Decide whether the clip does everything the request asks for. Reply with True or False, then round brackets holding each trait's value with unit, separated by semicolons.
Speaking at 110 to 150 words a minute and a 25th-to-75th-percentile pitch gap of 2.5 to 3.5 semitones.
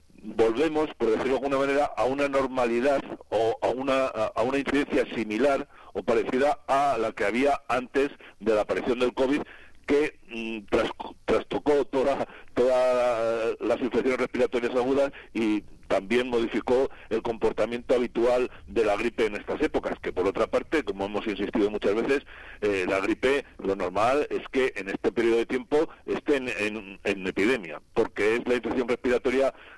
False (165 wpm; 2.8 semitones)